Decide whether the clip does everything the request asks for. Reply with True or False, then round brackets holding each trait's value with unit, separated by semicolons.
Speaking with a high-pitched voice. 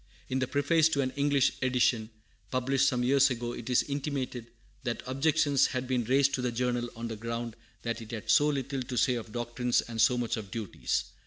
False (125 Hz)